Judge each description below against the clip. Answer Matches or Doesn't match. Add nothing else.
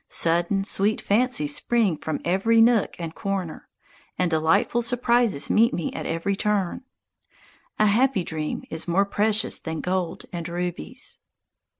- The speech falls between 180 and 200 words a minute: Doesn't match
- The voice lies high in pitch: Matches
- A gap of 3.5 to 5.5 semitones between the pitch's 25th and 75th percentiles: Matches